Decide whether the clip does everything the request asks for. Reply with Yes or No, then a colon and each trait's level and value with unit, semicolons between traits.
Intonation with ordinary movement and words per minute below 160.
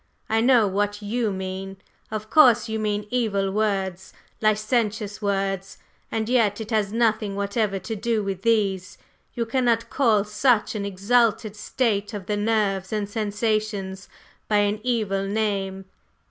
No: narrow, 2.1 semitones; average, 145 wpm